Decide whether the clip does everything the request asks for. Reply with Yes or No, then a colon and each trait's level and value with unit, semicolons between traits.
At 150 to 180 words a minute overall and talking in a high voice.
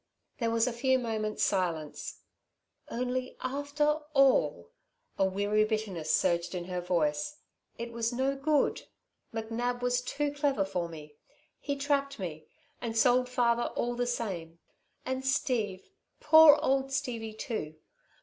No: slow, 135 wpm; high, 235 Hz